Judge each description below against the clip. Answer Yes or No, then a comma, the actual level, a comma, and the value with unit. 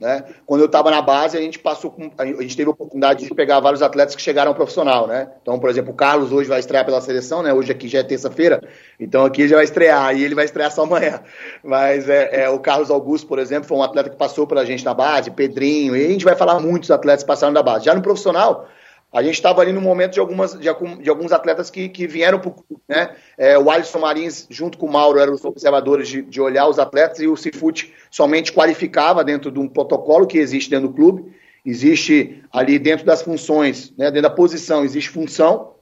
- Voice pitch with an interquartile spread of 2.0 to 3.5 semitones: Yes, average, 3.2 semitones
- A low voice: No, medium, 150 Hz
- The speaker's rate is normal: No, fast, 240 wpm